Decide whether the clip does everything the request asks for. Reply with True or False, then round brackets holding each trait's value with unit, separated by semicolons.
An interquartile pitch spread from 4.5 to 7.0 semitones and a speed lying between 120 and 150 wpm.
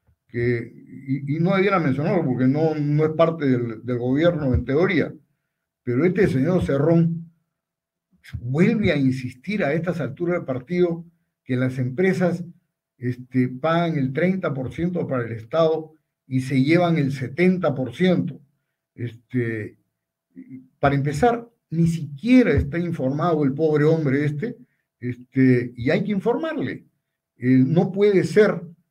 True (5.0 semitones; 130 wpm)